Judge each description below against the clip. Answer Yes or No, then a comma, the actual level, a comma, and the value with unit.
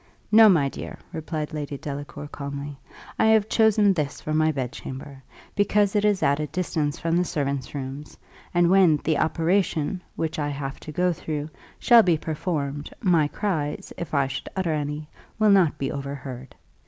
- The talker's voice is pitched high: No, medium, 155 Hz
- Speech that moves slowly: No, average, 170 wpm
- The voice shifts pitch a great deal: No, average, 4.1 semitones